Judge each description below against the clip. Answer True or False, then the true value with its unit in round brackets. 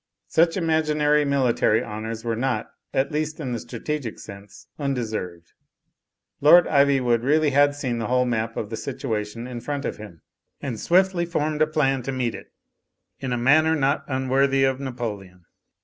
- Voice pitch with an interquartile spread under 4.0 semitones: False (4.3 semitones)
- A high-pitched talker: False (135 Hz)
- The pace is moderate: True (165 wpm)